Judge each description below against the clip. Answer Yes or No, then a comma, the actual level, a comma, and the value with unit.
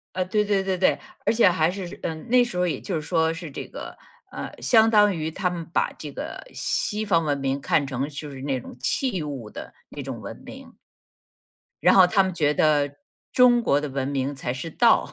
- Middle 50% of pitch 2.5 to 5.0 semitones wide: No, wide, 5.5 semitones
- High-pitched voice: No, medium, 165 Hz